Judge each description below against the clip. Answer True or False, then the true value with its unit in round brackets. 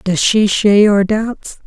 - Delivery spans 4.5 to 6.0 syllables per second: False (3.8 syllables/s)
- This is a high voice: True (205 Hz)